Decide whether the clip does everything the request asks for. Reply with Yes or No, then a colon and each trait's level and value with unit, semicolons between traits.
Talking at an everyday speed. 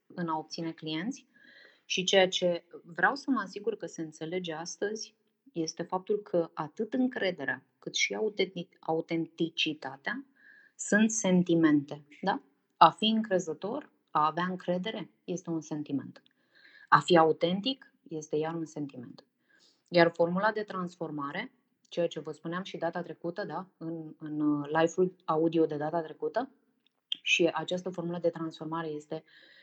Yes: average, 135 wpm